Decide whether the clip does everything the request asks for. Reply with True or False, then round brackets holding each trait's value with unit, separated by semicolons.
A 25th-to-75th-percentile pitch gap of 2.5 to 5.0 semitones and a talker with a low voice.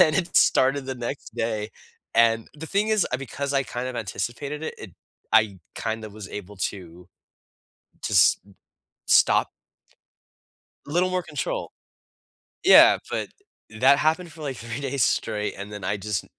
False (5.6 semitones; 120 Hz)